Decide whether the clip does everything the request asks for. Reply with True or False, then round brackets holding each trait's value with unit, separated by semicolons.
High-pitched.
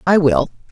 False (175 Hz)